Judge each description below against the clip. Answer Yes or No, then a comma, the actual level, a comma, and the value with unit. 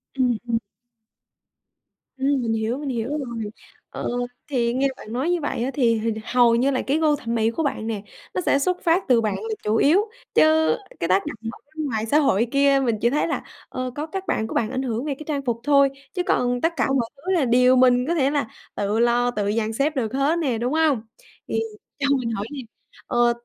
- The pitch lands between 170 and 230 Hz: No, very high, 255 Hz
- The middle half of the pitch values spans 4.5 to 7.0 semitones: No, average, 4.1 semitones